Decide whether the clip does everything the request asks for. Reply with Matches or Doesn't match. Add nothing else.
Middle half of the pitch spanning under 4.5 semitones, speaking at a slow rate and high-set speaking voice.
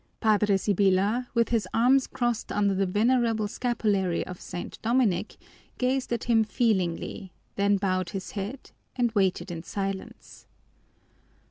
Matches